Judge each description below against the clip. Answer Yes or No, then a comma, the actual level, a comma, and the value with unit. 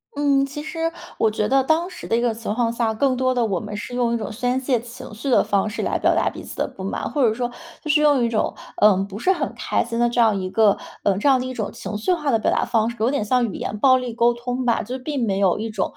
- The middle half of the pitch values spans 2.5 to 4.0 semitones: Yes, average, 3.2 semitones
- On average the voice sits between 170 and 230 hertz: No, high, 240 Hz